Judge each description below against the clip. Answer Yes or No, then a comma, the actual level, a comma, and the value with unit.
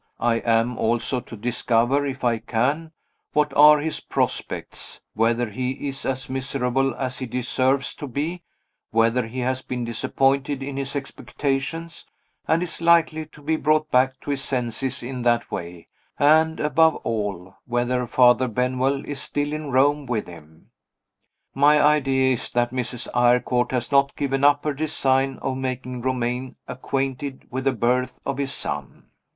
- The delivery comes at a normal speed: Yes, average, 155 wpm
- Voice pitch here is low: Yes, low, 130 Hz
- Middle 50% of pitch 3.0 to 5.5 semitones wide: No, narrow, 2.6 semitones